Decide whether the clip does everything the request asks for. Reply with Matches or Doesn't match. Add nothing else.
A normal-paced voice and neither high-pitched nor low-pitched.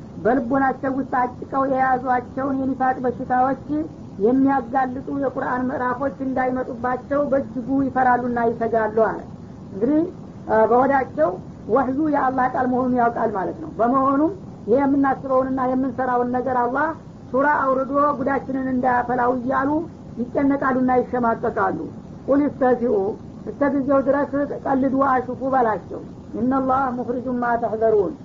Doesn't match